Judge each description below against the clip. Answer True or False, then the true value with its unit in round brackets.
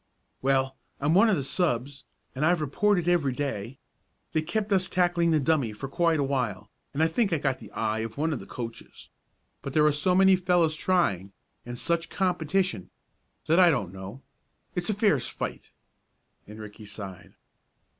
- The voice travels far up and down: True (6.4 semitones)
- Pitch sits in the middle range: True (150 Hz)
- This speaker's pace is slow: False (180 wpm)